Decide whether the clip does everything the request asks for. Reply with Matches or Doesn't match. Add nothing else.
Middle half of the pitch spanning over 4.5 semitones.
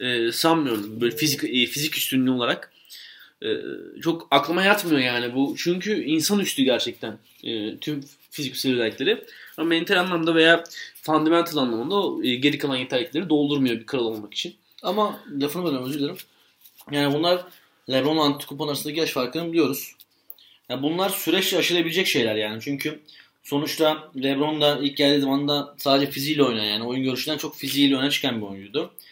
Doesn't match